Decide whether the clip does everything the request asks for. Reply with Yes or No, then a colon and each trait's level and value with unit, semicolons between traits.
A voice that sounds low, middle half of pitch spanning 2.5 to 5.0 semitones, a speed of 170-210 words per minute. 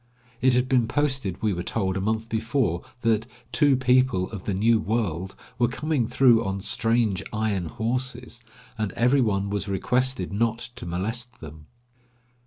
No: low, 115 Hz; average, 4.1 semitones; average, 160 wpm